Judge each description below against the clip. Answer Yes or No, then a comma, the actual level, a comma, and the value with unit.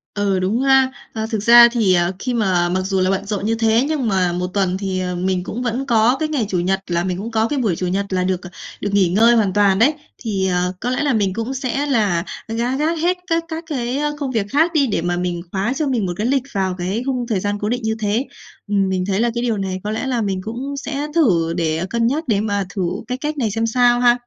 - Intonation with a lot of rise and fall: No, average, 4.9 semitones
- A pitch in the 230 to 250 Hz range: No, high, 220 Hz